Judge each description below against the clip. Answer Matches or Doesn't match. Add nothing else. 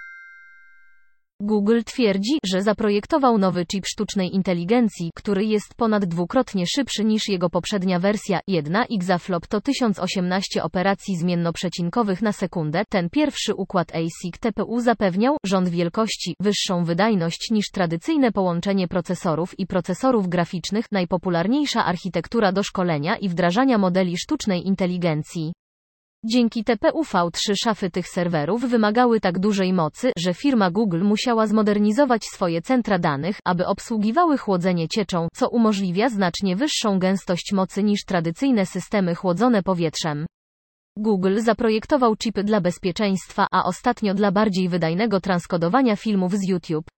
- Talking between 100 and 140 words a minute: Matches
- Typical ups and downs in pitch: Matches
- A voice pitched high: Matches